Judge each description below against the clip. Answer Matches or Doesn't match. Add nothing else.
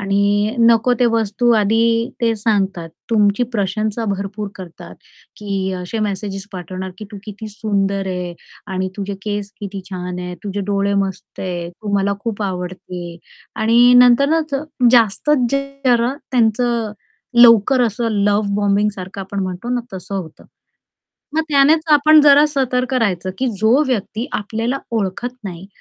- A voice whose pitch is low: Doesn't match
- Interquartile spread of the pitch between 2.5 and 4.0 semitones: Matches